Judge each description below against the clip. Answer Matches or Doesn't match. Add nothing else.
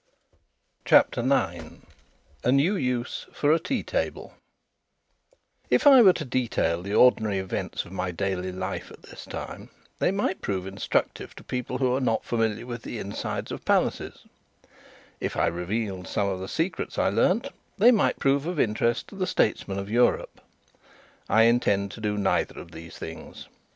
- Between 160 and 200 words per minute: Matches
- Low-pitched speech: Matches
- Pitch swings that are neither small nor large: Doesn't match